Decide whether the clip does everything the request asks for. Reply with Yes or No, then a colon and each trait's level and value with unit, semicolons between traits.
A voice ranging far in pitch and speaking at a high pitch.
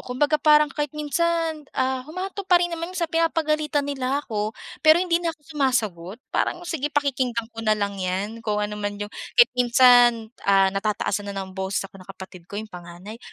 Yes: wide, 6.9 semitones; very high, 250 Hz